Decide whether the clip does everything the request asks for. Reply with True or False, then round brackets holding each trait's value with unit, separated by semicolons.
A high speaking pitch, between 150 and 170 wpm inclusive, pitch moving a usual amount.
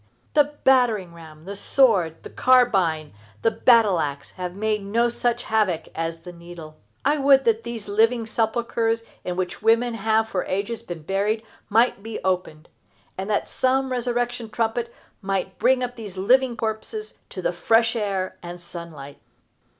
True (220 Hz; 160 wpm; 4.7 semitones)